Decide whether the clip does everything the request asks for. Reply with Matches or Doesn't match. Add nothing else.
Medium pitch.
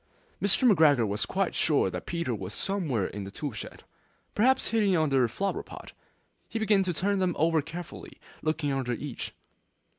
Matches